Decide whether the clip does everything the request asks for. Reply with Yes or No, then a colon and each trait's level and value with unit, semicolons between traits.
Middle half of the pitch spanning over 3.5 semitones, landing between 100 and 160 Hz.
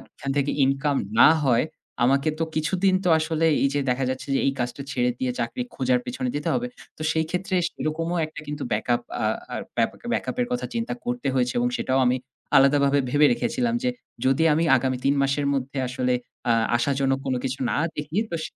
Yes: average, 4.1 semitones; medium, 140 Hz